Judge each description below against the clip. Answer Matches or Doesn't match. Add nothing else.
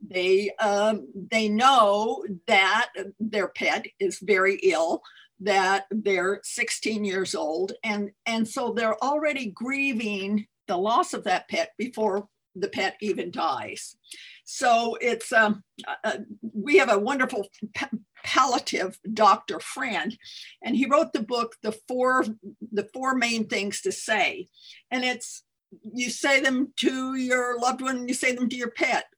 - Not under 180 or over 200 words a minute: Doesn't match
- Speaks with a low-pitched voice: Doesn't match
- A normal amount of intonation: Matches